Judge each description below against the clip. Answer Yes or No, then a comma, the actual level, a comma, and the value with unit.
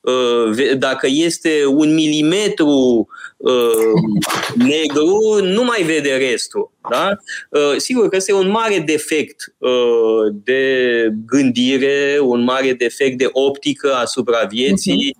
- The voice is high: No, medium, 140 Hz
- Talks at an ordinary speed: No, slow, 100 wpm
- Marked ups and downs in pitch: Yes, wide, 7.1 semitones